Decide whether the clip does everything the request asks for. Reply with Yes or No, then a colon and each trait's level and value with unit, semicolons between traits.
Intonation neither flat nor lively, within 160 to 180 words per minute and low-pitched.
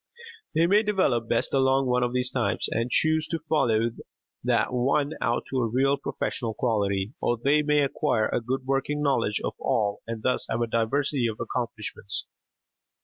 Yes: average, 3.5 semitones; average, 175 wpm; low, 125 Hz